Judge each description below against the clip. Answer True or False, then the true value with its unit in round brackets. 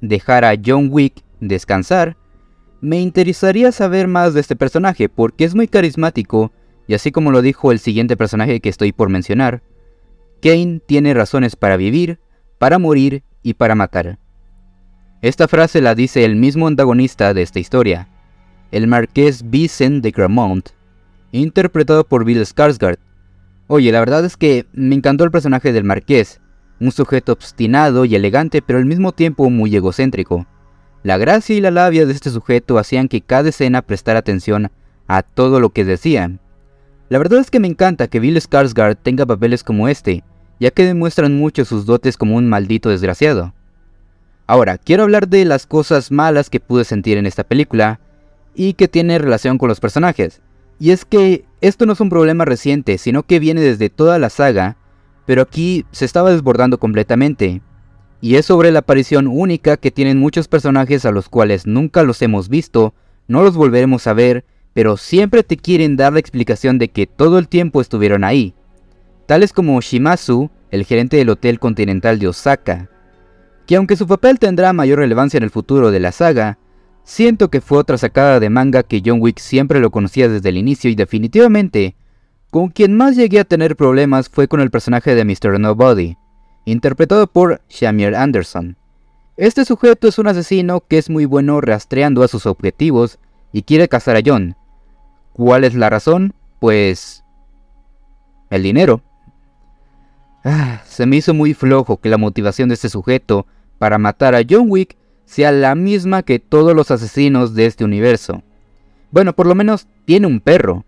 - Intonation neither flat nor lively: False (6.6 semitones)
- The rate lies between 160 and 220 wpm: True (170 wpm)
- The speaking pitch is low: True (125 Hz)